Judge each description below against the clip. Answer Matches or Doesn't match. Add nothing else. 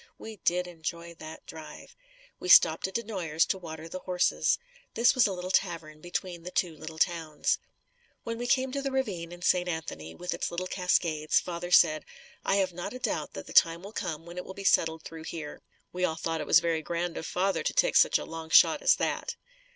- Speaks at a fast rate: Matches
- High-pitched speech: Doesn't match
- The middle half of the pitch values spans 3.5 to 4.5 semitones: Doesn't match